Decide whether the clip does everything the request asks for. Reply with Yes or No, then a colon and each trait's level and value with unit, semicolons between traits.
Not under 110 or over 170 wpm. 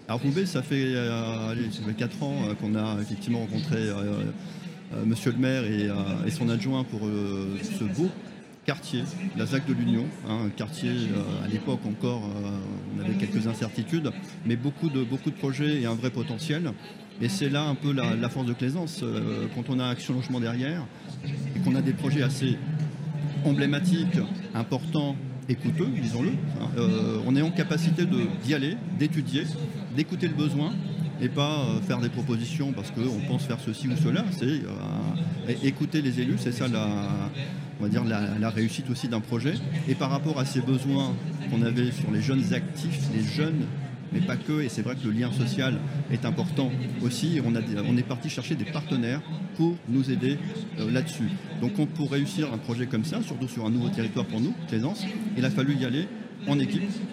No: average, 185 wpm